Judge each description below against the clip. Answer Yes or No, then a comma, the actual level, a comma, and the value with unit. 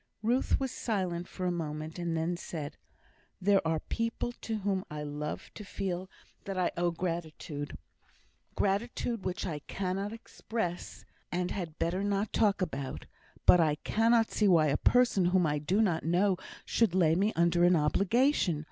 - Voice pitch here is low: No, medium, 180 Hz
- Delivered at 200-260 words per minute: No, average, 165 wpm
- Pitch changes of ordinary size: Yes, average, 3.7 semitones